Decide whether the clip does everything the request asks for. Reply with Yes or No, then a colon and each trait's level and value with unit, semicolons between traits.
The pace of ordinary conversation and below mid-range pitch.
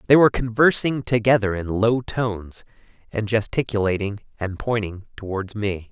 No: slow, 130 wpm; low, 110 Hz